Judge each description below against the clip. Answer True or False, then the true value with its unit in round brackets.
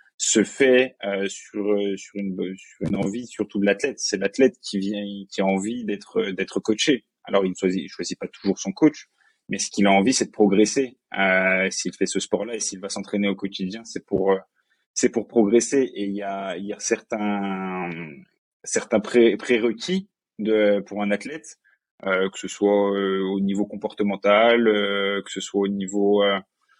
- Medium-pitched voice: False (100 Hz)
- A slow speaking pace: False (200 wpm)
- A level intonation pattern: True (1.8 semitones)